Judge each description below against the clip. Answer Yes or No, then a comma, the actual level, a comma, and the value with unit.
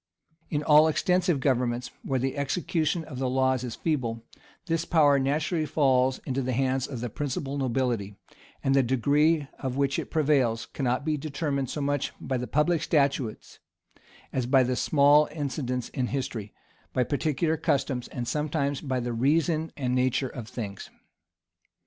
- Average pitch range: Yes, average, 3.0 semitones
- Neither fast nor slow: Yes, average, 155 wpm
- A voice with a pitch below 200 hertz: Yes, low, 135 Hz